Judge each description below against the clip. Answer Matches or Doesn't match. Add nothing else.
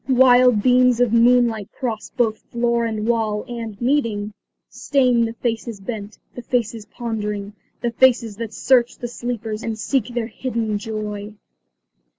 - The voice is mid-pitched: Doesn't match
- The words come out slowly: Doesn't match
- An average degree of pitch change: Doesn't match